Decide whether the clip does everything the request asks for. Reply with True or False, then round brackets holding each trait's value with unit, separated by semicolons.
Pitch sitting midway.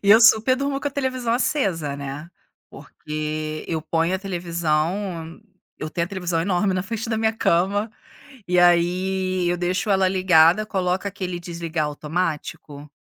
True (180 Hz)